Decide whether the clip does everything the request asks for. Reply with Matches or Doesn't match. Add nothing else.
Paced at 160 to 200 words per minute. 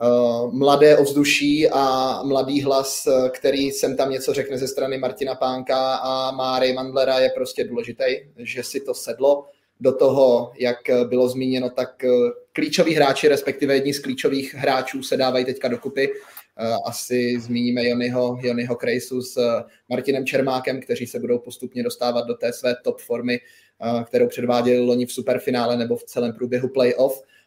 Doesn't match